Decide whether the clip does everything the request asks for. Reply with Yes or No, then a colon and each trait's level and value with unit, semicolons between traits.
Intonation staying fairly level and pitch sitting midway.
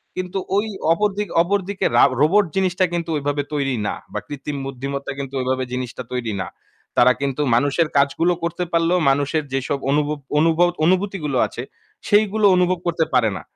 No: average, 4.8 semitones; medium, 155 Hz